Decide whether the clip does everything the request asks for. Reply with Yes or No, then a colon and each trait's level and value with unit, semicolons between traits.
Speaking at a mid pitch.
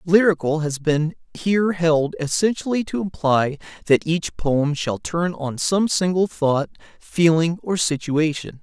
Yes: medium, 165 Hz